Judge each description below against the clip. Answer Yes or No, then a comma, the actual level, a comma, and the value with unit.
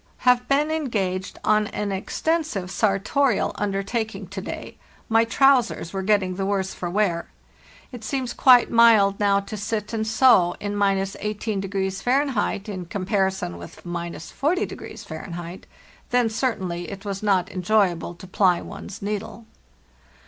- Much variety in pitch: No, average, 3.2 semitones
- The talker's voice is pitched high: Yes, high, 200 Hz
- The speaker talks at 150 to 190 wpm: No, slow, 135 wpm